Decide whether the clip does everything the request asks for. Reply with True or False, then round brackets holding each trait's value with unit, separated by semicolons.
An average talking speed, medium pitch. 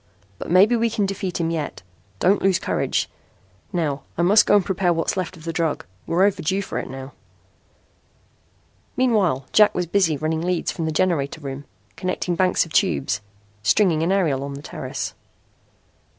True (170 wpm; 175 Hz)